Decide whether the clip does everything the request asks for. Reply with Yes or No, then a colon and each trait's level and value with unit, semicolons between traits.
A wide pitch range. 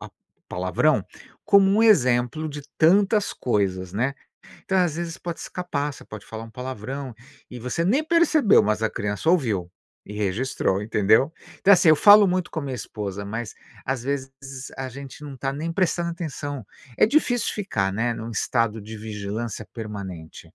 Yes: wide, 7.9 semitones